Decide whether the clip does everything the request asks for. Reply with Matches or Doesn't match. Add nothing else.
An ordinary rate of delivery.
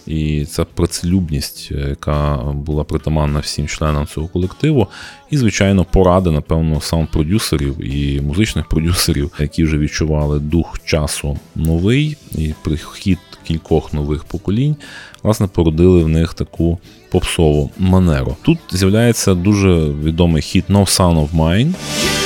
Matches